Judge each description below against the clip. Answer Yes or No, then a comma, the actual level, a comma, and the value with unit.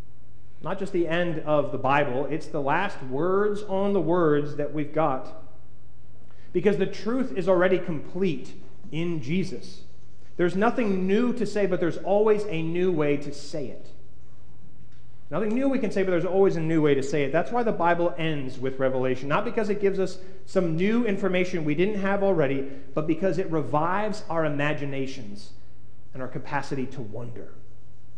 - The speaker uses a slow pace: No, average, 175 wpm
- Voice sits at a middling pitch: Yes, medium, 165 Hz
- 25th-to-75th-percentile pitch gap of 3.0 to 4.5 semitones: No, average, 5.1 semitones